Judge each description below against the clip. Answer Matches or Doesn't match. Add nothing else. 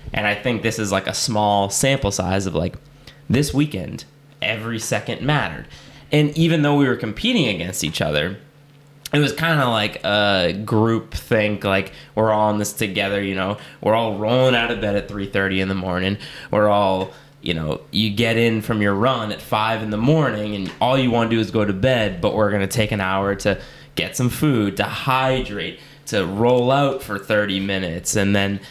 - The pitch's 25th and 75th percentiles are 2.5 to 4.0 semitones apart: Doesn't match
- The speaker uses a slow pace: Doesn't match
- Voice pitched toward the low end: Matches